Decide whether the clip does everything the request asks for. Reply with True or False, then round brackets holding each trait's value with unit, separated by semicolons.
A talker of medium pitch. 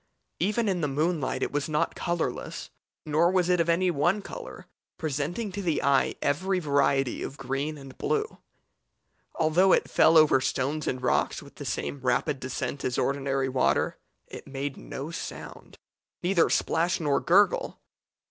True (150 Hz)